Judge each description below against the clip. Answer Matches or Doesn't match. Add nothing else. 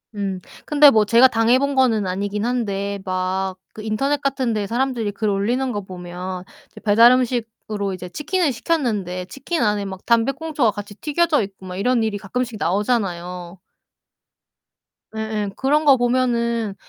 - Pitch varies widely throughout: Doesn't match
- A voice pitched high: Matches